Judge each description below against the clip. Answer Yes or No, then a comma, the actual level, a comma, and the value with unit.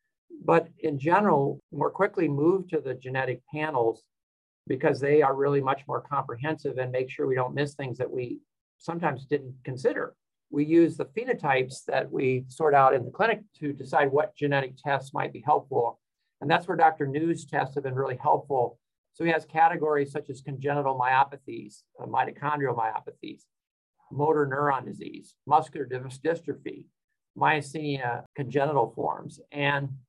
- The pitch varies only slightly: No, average, 3.1 semitones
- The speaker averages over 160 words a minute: No, average, 155 wpm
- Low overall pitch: No, medium, 145 Hz